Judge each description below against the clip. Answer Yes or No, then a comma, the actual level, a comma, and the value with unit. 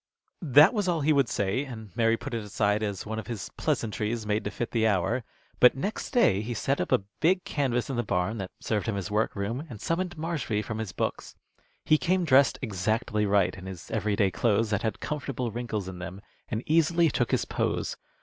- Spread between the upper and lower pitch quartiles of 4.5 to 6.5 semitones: Yes, average, 5.0 semitones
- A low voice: Yes, low, 115 Hz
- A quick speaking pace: Yes, fast, 215 wpm